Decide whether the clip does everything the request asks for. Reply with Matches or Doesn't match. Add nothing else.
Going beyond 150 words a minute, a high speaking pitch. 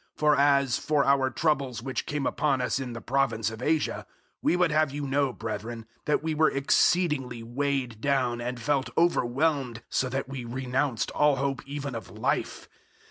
Doesn't match